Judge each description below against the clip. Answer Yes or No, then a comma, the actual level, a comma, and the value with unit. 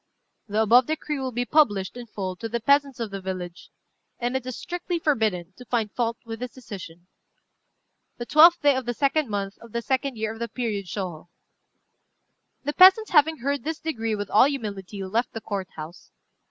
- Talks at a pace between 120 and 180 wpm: No, average, 195 wpm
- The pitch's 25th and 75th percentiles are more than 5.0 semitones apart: Yes, wide, 5.4 semitones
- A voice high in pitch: Yes, high, 235 Hz